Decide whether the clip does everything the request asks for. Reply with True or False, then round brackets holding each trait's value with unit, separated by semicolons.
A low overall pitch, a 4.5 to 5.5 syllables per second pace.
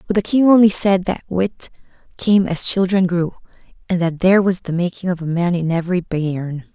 False (180 Hz; 5.3 syllables/s)